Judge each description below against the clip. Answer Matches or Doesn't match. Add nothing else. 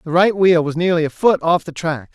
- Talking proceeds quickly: Matches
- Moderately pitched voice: Matches